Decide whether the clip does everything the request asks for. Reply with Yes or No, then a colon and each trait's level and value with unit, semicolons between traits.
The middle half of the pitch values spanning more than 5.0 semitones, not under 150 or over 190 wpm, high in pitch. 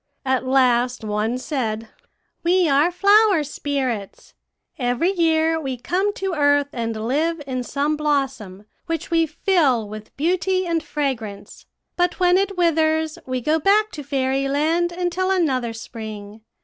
No: wide, 5.5 semitones; slow, 135 wpm; very high, 290 Hz